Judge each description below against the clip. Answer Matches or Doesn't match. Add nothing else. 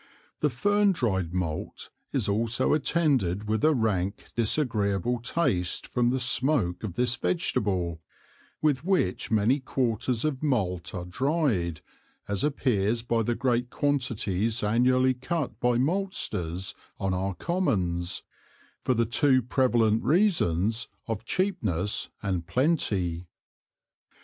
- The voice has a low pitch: Matches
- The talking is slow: Matches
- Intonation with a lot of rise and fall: Matches